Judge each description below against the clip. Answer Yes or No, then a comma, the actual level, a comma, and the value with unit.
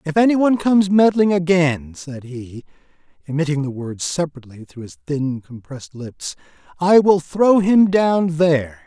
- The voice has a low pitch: No, medium, 160 Hz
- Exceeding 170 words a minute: No, average, 150 wpm